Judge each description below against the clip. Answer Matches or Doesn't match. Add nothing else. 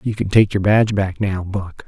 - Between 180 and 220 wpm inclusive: Doesn't match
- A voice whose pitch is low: Matches